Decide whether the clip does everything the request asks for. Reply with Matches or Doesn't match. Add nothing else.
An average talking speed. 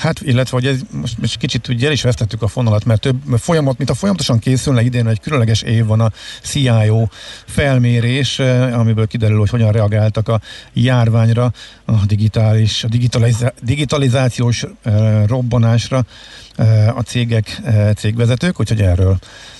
Matches